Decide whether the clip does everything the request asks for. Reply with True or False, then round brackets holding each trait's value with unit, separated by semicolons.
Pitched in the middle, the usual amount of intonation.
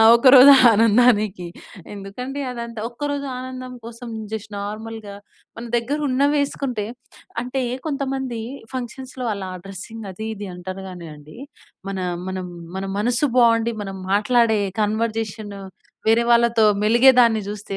False (230 Hz; 3.5 semitones)